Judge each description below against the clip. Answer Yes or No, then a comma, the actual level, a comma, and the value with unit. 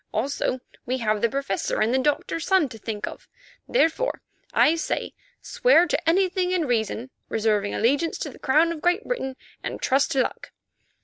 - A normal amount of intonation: No, wide, 6.5 semitones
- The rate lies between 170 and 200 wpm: Yes, average, 175 wpm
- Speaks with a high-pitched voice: Yes, very high, 275 Hz